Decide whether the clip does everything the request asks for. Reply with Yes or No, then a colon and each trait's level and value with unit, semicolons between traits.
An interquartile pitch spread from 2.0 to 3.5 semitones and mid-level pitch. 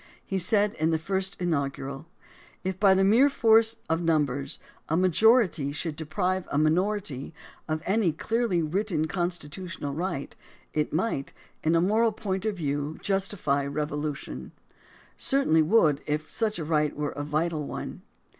No: average, 4.6 semitones; medium, 165 Hz